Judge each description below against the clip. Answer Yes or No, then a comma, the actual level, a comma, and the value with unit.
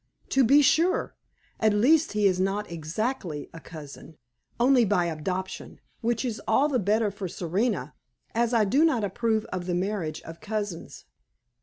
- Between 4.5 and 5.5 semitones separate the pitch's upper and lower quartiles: Yes, average, 5.1 semitones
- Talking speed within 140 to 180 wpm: Yes, average, 160 wpm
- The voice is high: Yes, high, 210 Hz